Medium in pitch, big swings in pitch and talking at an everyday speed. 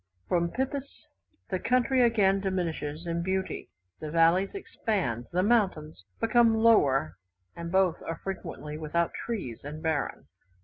No: medium, 180 Hz; wide, 6.0 semitones; slow, 130 wpm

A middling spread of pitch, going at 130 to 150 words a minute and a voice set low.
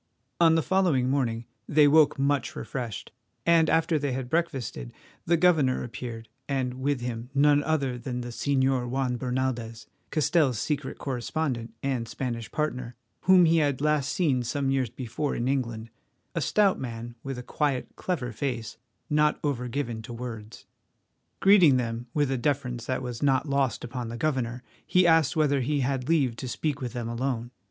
No: average, 3.4 semitones; average, 170 wpm; low, 130 Hz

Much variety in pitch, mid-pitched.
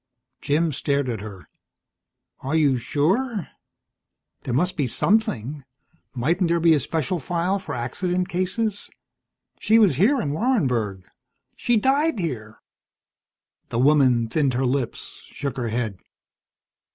Yes: wide, 6.8 semitones; medium, 150 Hz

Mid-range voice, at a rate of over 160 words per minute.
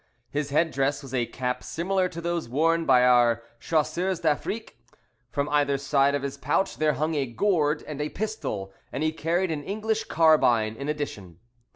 Yes: medium, 150 Hz; average, 180 wpm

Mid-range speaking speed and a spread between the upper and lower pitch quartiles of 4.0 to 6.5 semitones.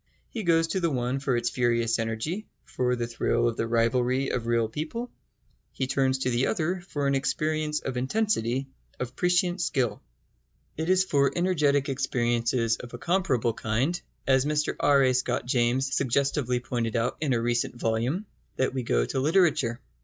Yes: average, 175 wpm; average, 4.3 semitones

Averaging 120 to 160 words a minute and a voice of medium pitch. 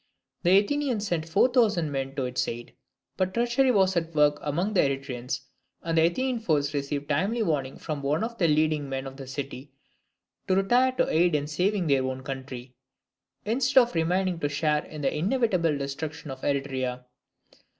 No: average, 180 wpm; medium, 155 Hz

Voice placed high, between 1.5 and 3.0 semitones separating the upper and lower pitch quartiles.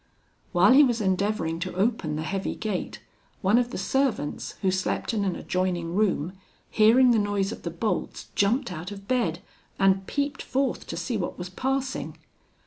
No: high, 200 Hz; average, 4.7 semitones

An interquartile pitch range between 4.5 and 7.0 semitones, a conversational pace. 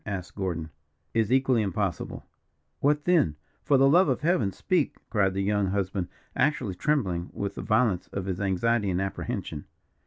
Yes: wide, 5.6 semitones; average, 160 wpm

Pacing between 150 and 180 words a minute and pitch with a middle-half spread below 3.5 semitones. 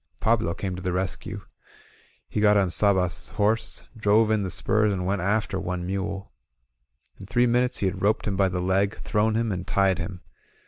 No: average, 190 wpm; narrow, 2.5 semitones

